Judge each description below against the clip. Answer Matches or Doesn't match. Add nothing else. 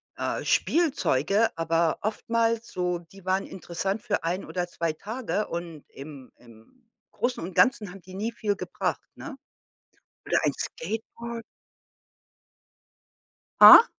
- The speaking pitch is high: Matches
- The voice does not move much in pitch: Doesn't match